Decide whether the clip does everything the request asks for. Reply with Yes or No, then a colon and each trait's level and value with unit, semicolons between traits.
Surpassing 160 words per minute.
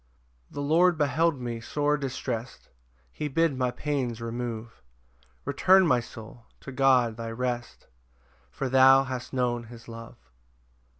No: slow, 135 wpm